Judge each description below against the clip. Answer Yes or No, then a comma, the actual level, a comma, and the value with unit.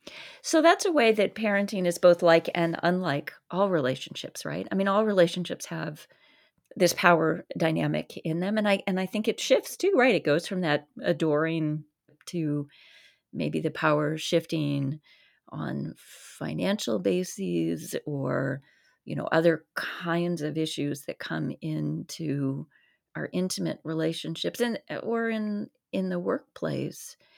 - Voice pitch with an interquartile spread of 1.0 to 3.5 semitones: No, average, 4.7 semitones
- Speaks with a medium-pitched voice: Yes, medium, 170 Hz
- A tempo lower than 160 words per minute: Yes, average, 140 wpm